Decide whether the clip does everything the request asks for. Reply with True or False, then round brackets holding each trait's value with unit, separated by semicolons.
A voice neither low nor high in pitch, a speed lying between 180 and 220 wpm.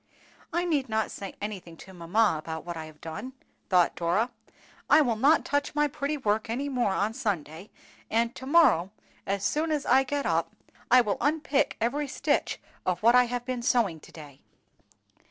False (230 Hz; 185 wpm)